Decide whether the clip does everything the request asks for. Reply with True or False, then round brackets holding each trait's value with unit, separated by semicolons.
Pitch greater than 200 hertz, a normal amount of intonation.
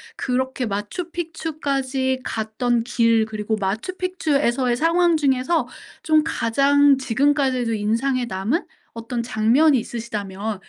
True (255 Hz; 4.4 semitones)